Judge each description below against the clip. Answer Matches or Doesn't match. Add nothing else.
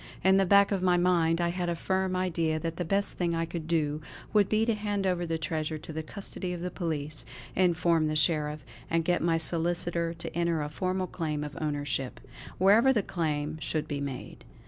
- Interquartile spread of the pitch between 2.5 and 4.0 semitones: Matches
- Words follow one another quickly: Matches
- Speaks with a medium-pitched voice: Matches